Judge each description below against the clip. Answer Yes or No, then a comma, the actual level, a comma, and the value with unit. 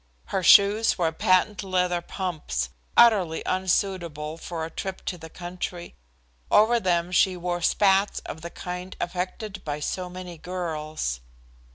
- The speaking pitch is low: No, medium, 180 Hz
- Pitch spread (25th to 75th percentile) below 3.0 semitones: Yes, narrow, 2.4 semitones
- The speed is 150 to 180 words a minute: No, average, 140 wpm